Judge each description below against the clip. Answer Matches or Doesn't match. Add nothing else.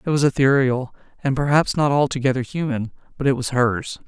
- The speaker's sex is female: Matches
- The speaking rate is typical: Matches